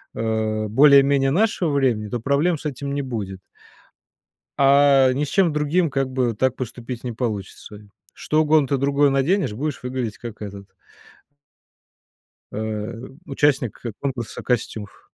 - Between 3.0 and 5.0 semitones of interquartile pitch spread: Yes, average, 4.1 semitones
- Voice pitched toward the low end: Yes, low, 130 Hz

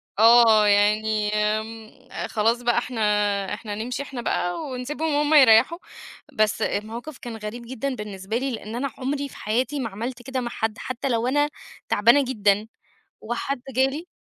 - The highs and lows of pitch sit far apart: No, average, 3.4 semitones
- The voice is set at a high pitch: Yes, high, 235 Hz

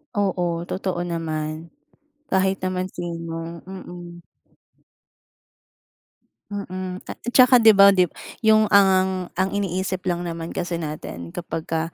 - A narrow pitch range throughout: Yes, narrow, 2.2 semitones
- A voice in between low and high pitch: Yes, medium, 180 Hz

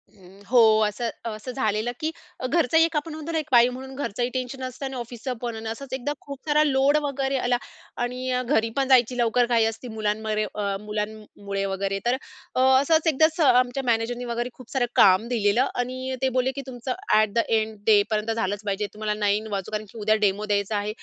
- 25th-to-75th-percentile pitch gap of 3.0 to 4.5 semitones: Yes, average, 3.6 semitones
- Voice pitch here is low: No, high, 235 Hz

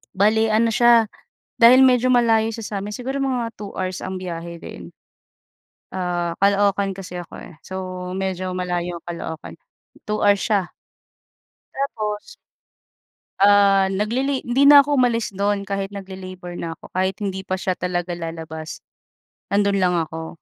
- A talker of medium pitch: No, high, 195 Hz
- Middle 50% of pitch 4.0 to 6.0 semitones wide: No, average, 3.5 semitones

